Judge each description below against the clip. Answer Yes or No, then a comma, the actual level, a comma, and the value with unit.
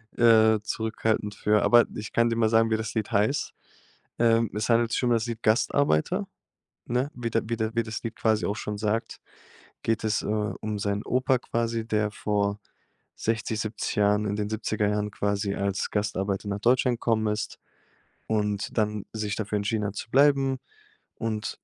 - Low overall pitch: Yes, low, 110 Hz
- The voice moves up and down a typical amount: No, narrow, 1.8 semitones